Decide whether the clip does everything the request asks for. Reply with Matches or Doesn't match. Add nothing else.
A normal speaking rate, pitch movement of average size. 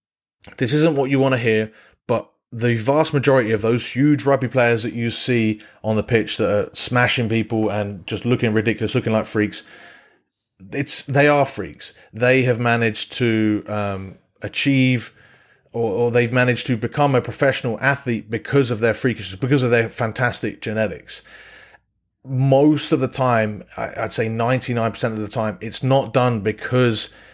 Matches